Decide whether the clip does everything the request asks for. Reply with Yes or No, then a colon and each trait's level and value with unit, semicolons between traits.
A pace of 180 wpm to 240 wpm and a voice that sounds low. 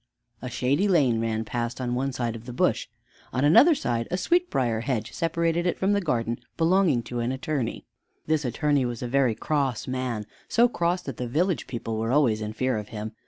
Yes: average, 200 wpm; low, 130 Hz